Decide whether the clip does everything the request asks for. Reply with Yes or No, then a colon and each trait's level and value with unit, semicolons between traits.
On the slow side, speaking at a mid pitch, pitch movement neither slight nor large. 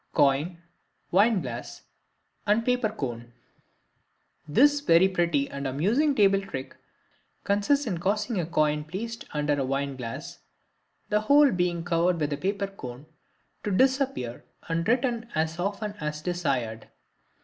No: slow, 130 wpm; medium, 175 Hz; wide, 6.5 semitones